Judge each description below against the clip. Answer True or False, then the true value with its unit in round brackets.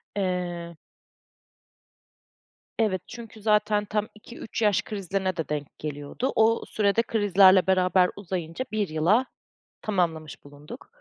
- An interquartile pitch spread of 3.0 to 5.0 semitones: True (3.8 semitones)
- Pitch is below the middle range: False (190 Hz)